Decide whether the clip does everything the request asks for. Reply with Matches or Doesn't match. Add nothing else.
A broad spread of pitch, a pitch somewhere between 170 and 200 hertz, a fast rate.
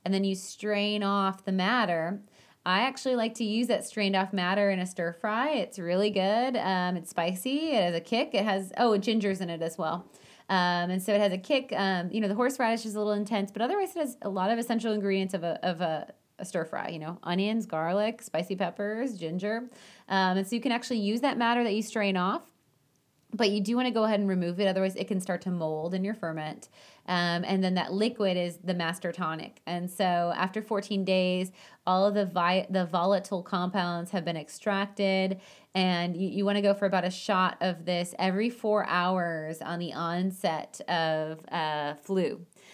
Doesn't match